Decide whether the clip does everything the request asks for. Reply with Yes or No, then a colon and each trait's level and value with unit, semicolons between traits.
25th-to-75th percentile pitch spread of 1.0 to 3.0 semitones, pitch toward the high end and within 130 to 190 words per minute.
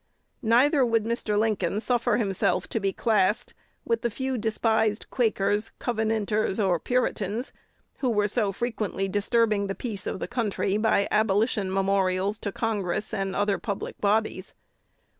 Yes: narrow, 2.5 semitones; high, 215 Hz; average, 140 wpm